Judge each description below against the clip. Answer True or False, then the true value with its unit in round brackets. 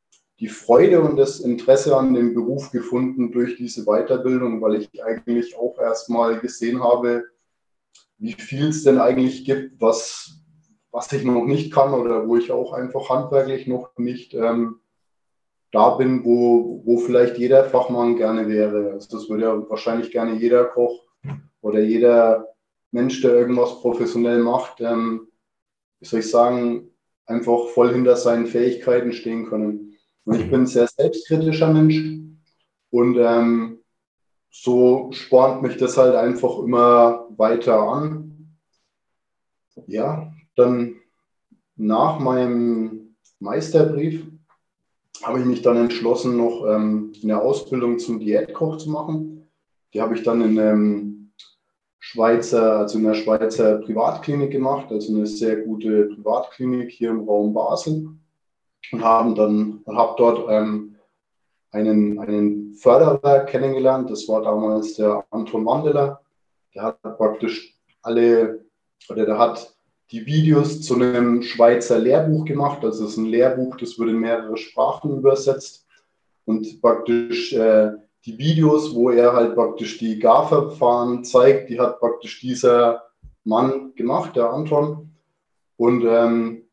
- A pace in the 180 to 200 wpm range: False (135 wpm)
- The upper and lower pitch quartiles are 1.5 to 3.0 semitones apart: True (2.7 semitones)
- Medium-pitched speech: False (120 Hz)